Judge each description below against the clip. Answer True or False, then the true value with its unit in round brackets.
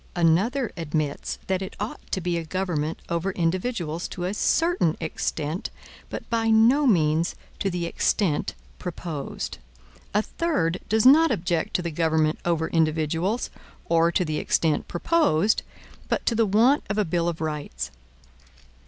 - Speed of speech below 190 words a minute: True (150 wpm)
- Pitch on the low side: False (175 Hz)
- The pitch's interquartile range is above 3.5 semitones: True (4.7 semitones)